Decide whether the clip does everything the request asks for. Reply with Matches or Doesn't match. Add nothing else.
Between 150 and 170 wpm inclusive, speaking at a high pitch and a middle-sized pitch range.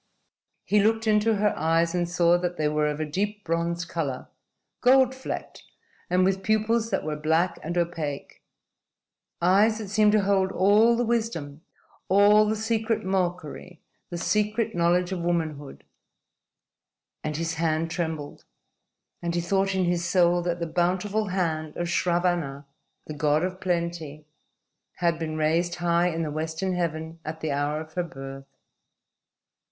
Doesn't match